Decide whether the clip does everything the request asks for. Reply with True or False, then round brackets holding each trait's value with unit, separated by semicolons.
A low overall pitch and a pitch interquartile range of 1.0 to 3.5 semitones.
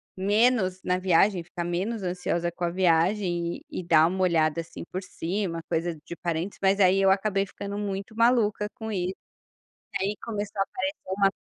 False (190 Hz; 2.9 semitones)